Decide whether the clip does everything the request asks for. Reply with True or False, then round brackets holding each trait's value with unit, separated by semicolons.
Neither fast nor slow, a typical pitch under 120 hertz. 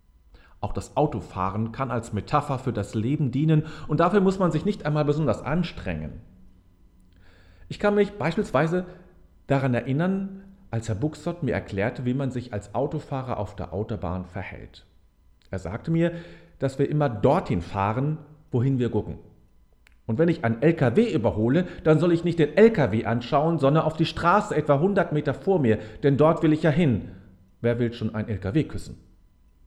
False (170 wpm; 125 Hz)